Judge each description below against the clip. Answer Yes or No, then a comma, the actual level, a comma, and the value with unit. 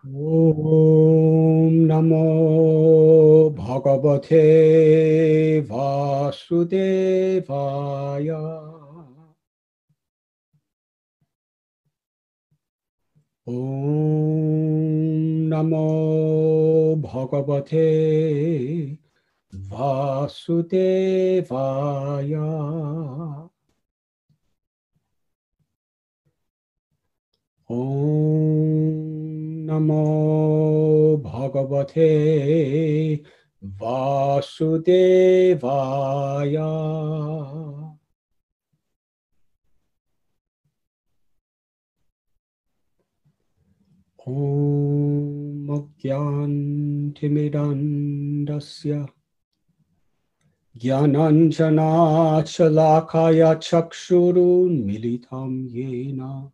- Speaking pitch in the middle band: Yes, medium, 155 Hz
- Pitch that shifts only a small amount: Yes, narrow, 2.2 semitones